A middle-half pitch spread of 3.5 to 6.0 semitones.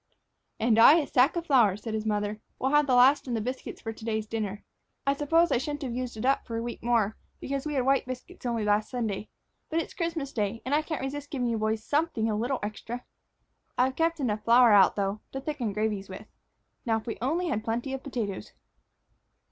Yes: average, 4.2 semitones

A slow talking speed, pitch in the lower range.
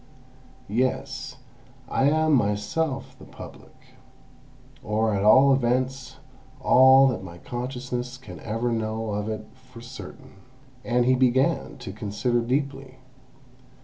Yes: slow, 115 wpm; low, 125 Hz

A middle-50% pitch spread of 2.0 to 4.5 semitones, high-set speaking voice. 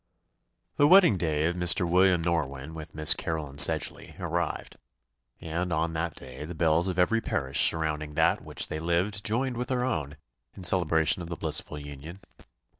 No: average, 2.9 semitones; very low, 85 Hz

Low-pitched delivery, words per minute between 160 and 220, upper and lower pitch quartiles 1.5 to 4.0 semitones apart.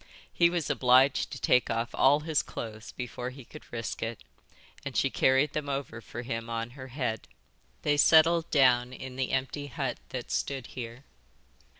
Yes: low, 130 Hz; average, 175 wpm; average, 3.2 semitones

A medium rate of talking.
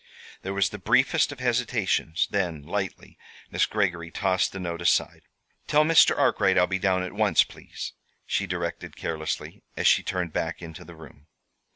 Yes: average, 170 wpm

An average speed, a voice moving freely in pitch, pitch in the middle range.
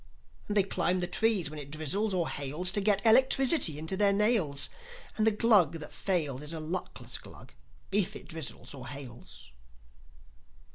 Yes: average, 170 wpm; wide, 5.7 semitones; medium, 180 Hz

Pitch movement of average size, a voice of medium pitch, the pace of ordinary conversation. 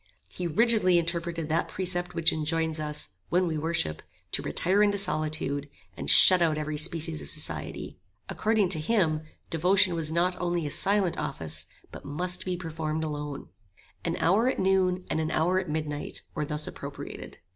Yes: average, 3.0 semitones; medium, 165 Hz; average, 165 wpm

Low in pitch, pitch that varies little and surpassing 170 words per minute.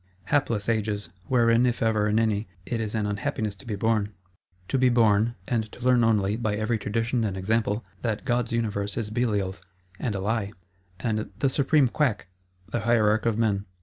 Yes: low, 110 Hz; narrow, 2.2 semitones; average, 180 wpm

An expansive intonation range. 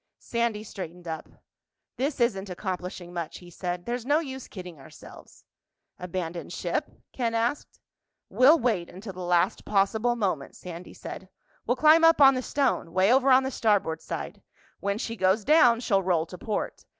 Yes: wide, 5.7 semitones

